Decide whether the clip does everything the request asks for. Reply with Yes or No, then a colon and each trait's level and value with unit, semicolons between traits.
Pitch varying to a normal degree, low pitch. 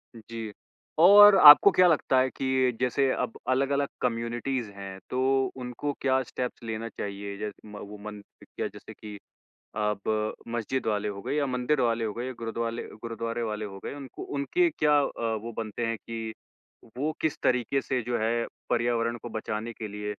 Yes: average, 3.3 semitones; low, 115 Hz